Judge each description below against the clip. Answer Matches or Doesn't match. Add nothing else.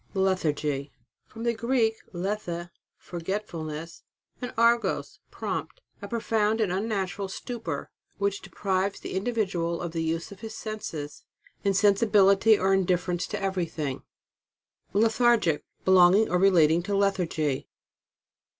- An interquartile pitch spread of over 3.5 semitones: Matches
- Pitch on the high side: Matches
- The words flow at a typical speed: Doesn't match